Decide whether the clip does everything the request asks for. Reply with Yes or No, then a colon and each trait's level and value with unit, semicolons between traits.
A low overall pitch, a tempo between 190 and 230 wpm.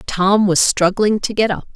No: high, 200 Hz; fast, 205 wpm